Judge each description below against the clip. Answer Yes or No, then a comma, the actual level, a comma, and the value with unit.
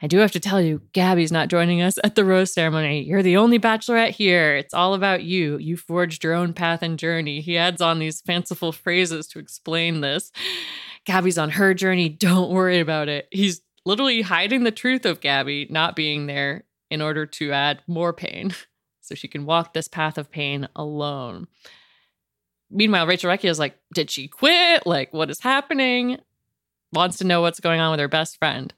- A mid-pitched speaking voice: Yes, medium, 170 Hz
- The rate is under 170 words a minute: No, average, 195 wpm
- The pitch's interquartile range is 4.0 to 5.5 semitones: No, average, 3.5 semitones